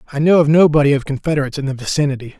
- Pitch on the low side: No, medium, 145 Hz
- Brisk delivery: Yes, fast, 250 wpm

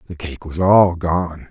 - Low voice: Yes, very low, 85 Hz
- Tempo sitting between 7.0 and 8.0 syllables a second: No, 3.8 syllables/s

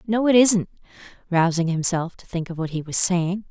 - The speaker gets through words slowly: No, fast, 205 wpm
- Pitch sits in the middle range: Yes, medium, 180 Hz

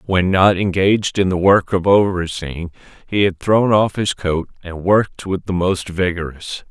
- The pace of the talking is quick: No, average, 180 wpm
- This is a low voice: Yes, very low, 95 Hz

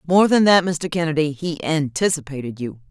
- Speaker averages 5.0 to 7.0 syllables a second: Yes, 5.3 syllables/s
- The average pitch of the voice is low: No, medium, 160 Hz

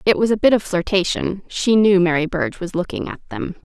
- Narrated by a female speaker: Yes, female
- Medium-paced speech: No, fast, 210 wpm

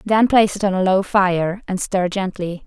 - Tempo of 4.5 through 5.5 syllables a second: Yes, 4.8 syllables/s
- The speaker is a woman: Yes, female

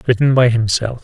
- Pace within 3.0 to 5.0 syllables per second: No, 5.6 syllables/s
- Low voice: Yes, low, 120 Hz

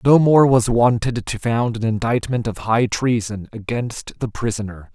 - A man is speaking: Yes, male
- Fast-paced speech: No, average, 170 wpm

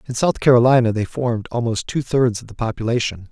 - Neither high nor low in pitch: No, low, 115 Hz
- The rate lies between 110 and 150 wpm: No, average, 200 wpm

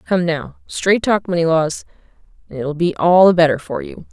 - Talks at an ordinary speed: Yes, average, 160 wpm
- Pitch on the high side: No, medium, 170 Hz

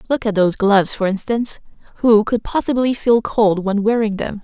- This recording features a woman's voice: Yes, female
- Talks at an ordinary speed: Yes, average, 190 wpm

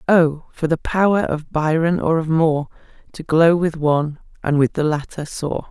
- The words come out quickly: No, average, 190 wpm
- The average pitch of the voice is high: No, medium, 160 Hz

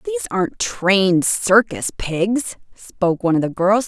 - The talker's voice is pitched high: Yes, high, 195 Hz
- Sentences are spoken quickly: No, average, 155 wpm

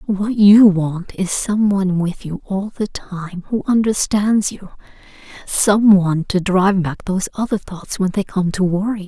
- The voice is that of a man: No, female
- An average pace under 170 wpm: No, average, 185 wpm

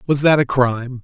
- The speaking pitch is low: Yes, low, 130 Hz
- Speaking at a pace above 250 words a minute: No, fast, 235 wpm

